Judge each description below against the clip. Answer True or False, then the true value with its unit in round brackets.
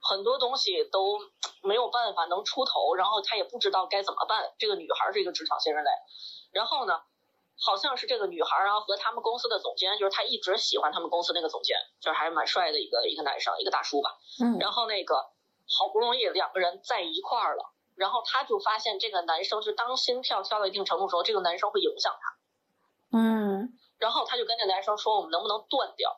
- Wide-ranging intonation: True (5.7 semitones)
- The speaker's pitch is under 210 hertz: False (220 Hz)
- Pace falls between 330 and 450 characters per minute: True (350 characters per minute)